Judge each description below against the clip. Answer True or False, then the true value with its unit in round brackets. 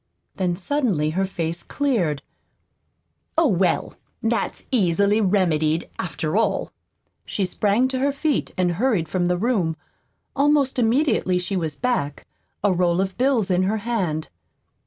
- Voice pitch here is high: True (195 Hz)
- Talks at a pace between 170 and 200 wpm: False (135 wpm)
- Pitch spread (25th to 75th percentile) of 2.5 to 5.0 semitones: False (5.6 semitones)